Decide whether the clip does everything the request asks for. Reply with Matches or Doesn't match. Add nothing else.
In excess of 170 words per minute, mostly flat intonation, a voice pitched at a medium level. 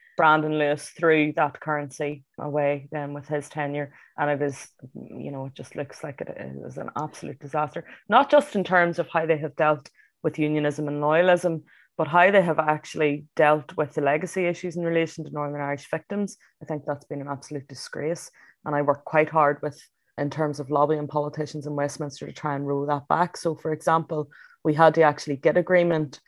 Matches